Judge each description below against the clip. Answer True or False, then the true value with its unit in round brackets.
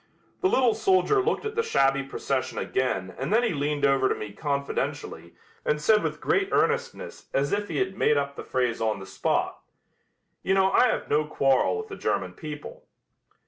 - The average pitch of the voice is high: False (150 Hz)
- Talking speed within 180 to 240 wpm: True (190 wpm)